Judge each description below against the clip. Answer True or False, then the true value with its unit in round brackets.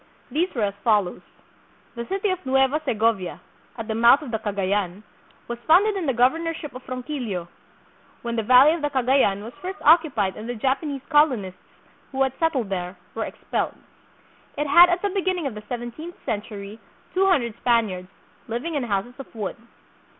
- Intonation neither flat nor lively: False (6.1 semitones)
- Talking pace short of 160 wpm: False (170 wpm)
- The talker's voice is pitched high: True (250 Hz)